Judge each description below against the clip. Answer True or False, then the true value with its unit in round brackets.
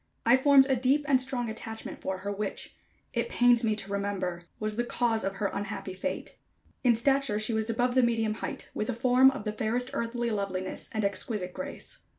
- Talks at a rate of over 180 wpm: True (200 wpm)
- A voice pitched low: False (225 Hz)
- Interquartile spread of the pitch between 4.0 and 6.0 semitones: False (3.6 semitones)